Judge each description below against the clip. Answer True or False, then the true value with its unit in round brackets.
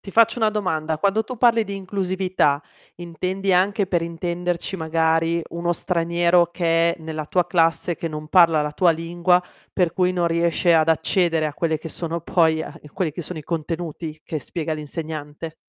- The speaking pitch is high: False (170 Hz)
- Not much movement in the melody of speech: True (2.2 semitones)